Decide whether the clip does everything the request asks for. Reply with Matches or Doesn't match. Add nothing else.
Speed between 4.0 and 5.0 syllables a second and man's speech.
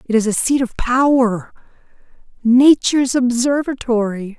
Doesn't match